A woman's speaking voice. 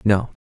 No: male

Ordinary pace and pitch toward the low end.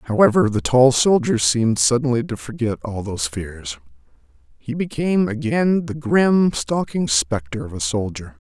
Yes: average, 150 wpm; low, 125 Hz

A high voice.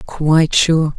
No: medium, 160 Hz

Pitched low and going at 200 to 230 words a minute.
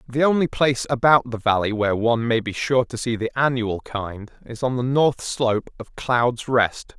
Yes: low, 120 Hz; fast, 205 wpm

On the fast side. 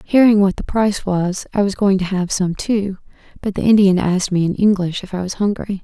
Yes: fast, 235 wpm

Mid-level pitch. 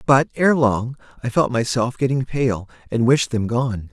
No: low, 120 Hz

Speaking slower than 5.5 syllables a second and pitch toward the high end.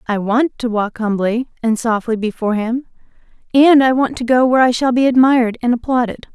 No: 5.6 syllables/s; high, 240 Hz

